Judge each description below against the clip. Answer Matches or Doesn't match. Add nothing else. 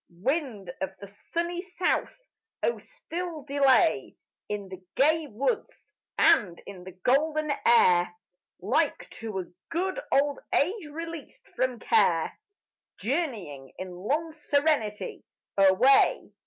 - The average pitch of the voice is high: Matches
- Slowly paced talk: Matches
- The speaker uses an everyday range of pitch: Doesn't match